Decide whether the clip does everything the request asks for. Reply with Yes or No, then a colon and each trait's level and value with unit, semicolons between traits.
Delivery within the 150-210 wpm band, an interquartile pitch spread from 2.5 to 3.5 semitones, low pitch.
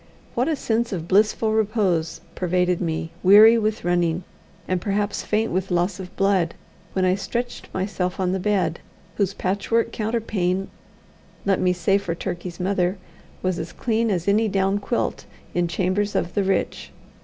No: average, 160 wpm; average, 2.8 semitones; high, 190 Hz